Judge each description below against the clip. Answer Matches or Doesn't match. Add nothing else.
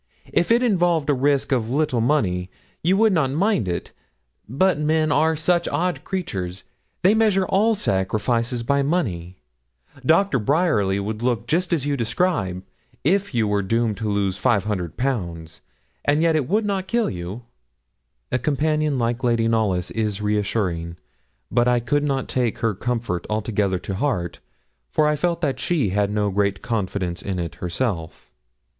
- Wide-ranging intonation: Matches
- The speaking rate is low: Doesn't match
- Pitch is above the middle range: Doesn't match